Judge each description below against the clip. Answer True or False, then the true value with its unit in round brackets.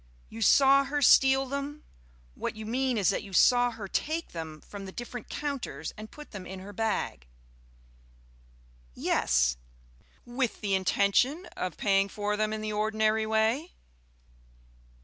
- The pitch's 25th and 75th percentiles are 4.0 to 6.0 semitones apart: True (4.9 semitones)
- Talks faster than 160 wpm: False (150 wpm)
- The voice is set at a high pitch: True (220 Hz)